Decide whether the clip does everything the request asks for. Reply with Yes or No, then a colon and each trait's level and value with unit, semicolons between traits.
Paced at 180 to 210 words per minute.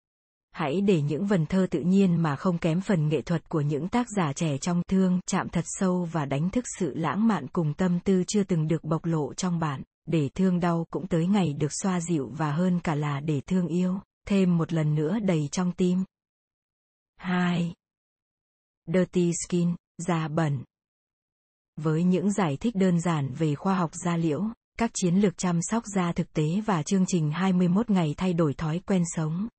Yes: average, 195 wpm